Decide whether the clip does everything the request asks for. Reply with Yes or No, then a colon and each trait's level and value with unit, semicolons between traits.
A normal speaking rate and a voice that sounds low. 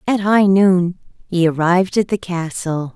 No: average, 160 wpm; medium, 180 Hz